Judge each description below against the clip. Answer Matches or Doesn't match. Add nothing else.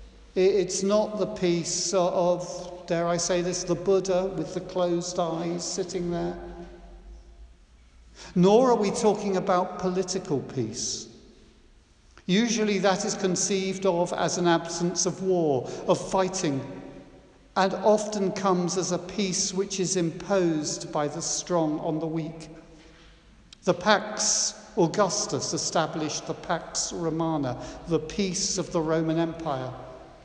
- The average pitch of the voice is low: Doesn't match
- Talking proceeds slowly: Matches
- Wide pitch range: Doesn't match